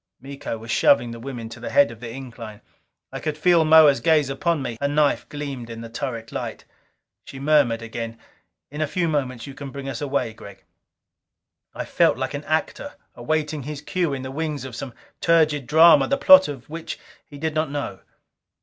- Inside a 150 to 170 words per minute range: No, average, 195 wpm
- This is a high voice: No, medium, 140 Hz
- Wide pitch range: No, average, 4.2 semitones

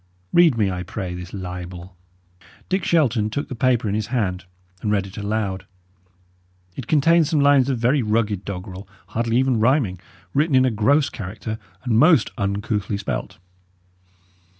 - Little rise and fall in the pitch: No, average, 5.2 semitones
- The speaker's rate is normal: Yes, average, 155 wpm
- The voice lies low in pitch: Yes, low, 110 Hz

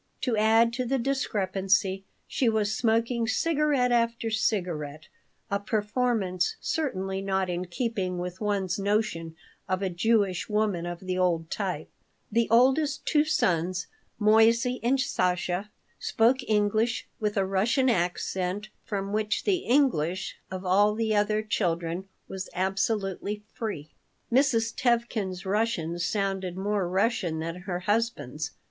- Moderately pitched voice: No, high, 205 Hz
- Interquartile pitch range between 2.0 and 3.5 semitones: No, average, 3.9 semitones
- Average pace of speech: No, slow, 130 wpm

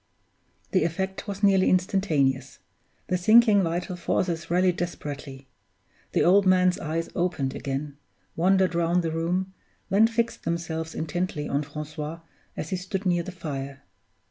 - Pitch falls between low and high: Yes, medium, 175 Hz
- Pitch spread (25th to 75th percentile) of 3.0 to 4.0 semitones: Yes, average, 3.4 semitones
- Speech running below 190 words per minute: Yes, average, 140 wpm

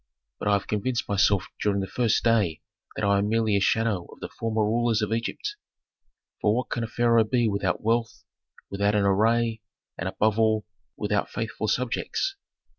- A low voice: Yes, low, 110 Hz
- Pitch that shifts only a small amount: Yes, narrow, 2.2 semitones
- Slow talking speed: No, average, 180 wpm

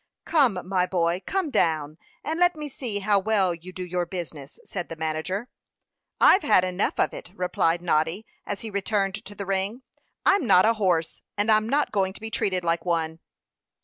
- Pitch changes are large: No, average, 4.0 semitones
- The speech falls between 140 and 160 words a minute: No, average, 190 wpm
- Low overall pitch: No, high, 190 Hz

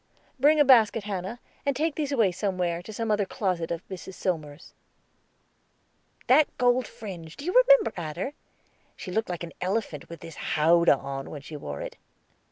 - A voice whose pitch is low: No, high, 190 Hz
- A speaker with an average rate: Yes, average, 175 wpm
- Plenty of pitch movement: Yes, wide, 6.6 semitones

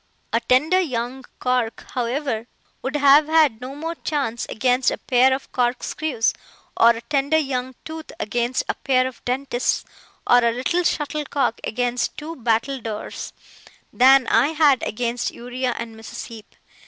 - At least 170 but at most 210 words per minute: No, average, 145 wpm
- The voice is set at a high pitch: Yes, very high, 255 Hz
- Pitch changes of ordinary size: Yes, average, 3.0 semitones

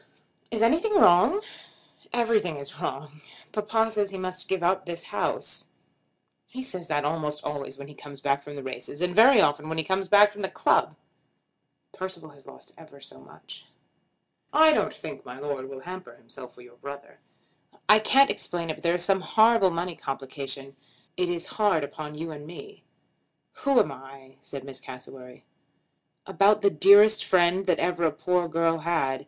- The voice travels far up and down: Yes, wide, 5.7 semitones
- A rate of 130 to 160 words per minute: No, average, 180 wpm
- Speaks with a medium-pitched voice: Yes, medium, 170 Hz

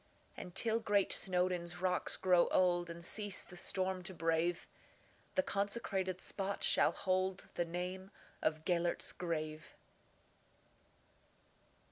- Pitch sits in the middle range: Yes, medium, 180 Hz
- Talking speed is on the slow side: Yes, slow, 100 wpm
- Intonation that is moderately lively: No, narrow, 1.7 semitones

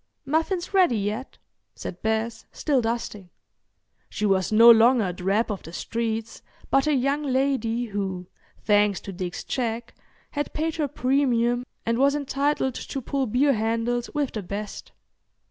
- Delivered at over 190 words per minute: No, average, 150 wpm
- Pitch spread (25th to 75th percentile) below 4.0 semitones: No, average, 4.4 semitones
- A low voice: No, high, 235 Hz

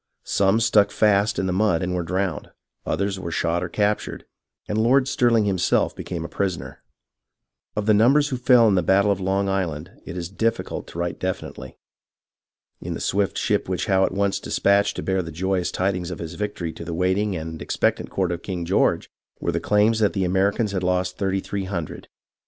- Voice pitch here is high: No, very low, 95 Hz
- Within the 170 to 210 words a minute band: Yes, average, 200 wpm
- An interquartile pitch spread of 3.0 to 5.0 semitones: No, narrow, 2.5 semitones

